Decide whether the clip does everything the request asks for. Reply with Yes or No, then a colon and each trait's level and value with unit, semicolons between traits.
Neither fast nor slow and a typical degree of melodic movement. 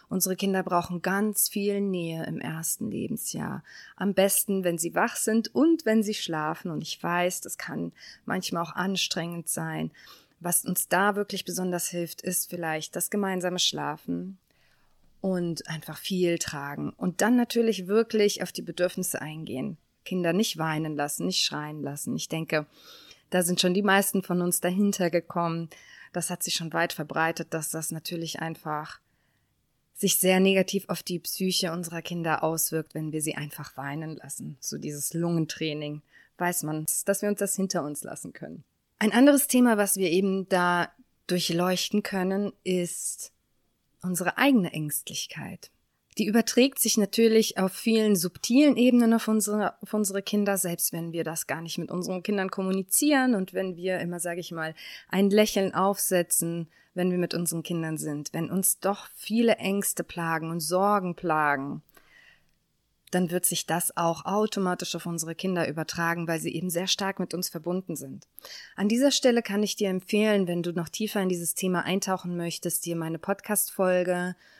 Yes: average, 165 wpm; average, 3.2 semitones